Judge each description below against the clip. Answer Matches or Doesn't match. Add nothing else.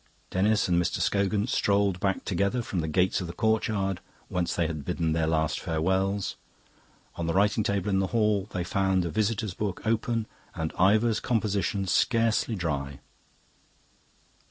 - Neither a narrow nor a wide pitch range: Matches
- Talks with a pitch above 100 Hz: Doesn't match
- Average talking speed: Matches